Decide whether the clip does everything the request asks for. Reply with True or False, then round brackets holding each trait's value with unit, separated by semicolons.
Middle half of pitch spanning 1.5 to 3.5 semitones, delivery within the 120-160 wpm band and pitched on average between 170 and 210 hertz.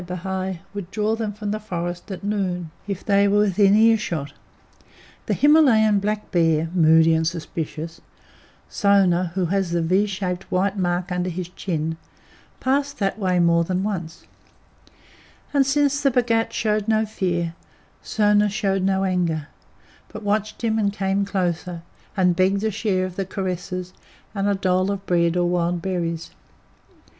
True (3.0 semitones; 155 wpm; 190 Hz)